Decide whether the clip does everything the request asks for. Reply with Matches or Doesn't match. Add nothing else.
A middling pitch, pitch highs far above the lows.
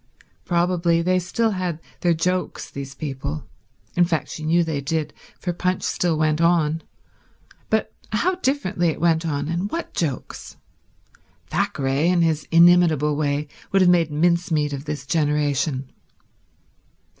Doesn't match